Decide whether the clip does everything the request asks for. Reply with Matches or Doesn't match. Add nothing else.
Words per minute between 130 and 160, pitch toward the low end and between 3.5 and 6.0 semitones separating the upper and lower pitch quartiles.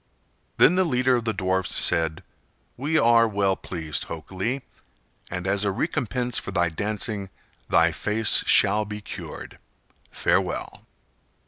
Matches